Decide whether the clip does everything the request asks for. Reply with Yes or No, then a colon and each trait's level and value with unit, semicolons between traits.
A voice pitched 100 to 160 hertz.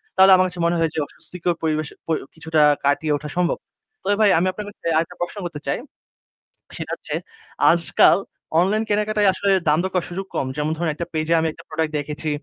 No: medium, 170 Hz